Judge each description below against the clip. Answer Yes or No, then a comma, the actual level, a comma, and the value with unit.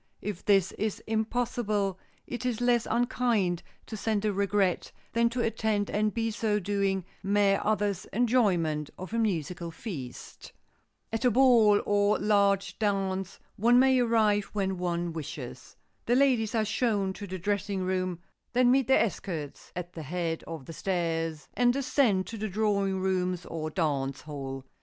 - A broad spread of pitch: No, average, 3.8 semitones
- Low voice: No, high, 200 Hz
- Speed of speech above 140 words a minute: Yes, average, 155 wpm